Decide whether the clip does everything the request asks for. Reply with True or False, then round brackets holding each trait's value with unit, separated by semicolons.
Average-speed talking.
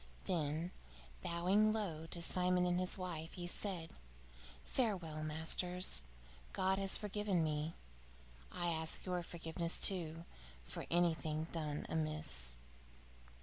False (110 wpm)